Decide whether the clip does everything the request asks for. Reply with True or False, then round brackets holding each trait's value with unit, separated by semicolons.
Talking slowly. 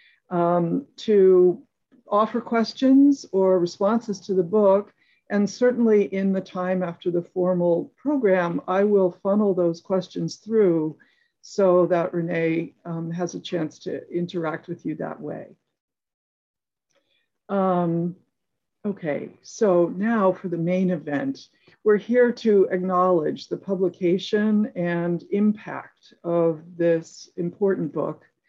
True (120 wpm)